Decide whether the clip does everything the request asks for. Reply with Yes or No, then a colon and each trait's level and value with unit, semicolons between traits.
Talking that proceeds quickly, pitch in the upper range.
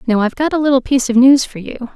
Yes: fast, 305 wpm; very high, 255 Hz